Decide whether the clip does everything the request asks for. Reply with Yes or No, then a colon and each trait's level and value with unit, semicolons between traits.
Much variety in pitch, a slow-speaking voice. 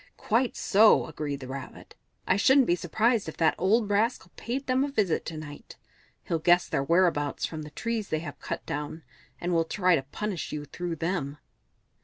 No: wide, 5.9 semitones; average, 190 wpm